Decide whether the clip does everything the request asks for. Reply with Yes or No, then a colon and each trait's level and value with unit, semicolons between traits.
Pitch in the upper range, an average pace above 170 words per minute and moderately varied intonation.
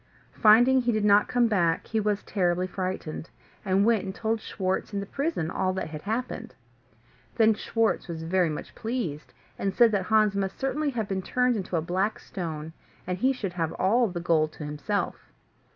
Yes: high, 200 Hz; average, 190 wpm; average, 4.1 semitones